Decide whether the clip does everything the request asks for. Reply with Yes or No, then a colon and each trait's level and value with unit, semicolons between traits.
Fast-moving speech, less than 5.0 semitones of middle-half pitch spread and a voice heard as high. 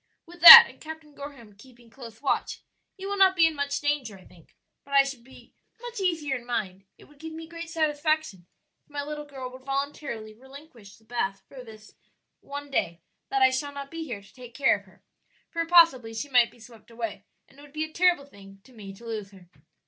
No: fast, 225 wpm; wide, 5.4 semitones; very high, 275 Hz